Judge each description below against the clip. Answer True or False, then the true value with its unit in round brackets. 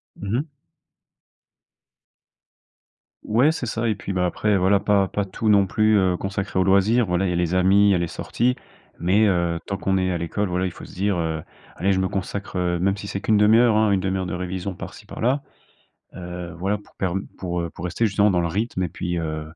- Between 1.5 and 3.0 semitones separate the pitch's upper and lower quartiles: True (2.6 semitones)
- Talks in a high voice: False (95 Hz)